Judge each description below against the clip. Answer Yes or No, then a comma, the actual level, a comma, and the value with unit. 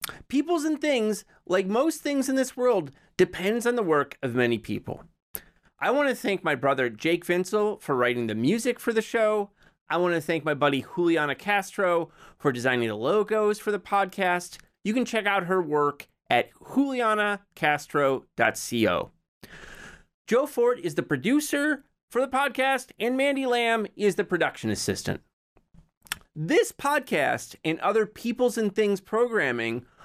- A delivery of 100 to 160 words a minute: Yes, average, 155 wpm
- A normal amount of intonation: No, wide, 7.2 semitones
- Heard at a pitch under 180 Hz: No, high, 200 Hz